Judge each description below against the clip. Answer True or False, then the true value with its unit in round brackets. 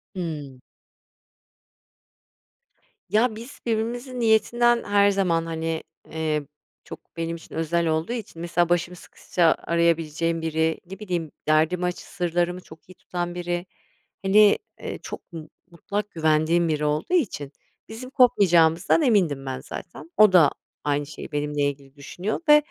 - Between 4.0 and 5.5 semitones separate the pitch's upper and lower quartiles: True (4.3 semitones)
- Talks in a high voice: False (170 Hz)